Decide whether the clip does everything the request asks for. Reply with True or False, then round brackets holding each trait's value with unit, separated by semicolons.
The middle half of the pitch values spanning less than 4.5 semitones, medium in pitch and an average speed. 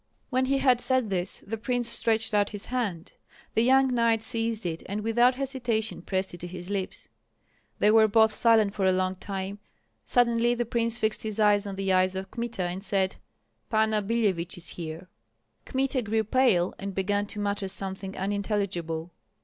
False (3.4 semitones; 210 Hz; 180 wpm)